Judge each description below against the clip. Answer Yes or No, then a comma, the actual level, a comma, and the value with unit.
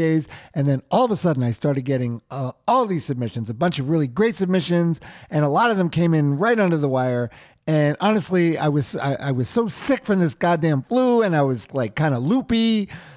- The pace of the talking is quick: Yes, fast, 230 wpm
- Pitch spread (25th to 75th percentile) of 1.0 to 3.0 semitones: No, wide, 5.5 semitones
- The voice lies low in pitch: No, medium, 155 Hz